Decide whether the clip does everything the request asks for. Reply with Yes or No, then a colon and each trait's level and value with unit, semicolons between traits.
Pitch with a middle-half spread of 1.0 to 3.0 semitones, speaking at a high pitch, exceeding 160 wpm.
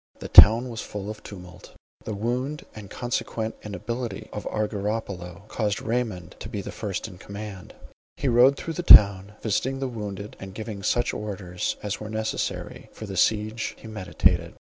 No: average, 2.7 semitones; low, 105 Hz; average, 170 wpm